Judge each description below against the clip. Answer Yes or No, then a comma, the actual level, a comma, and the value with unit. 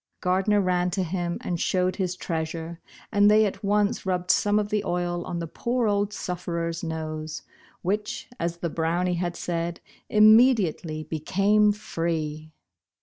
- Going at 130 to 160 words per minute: Yes, average, 150 wpm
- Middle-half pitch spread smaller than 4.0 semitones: Yes, average, 3.5 semitones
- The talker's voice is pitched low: No, medium, 180 Hz